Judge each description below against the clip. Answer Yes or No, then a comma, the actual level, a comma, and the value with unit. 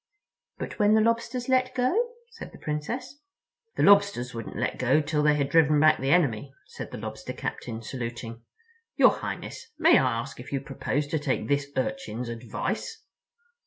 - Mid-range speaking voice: Yes, medium, 150 Hz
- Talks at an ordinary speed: Yes, average, 170 wpm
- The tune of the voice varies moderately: No, wide, 8.9 semitones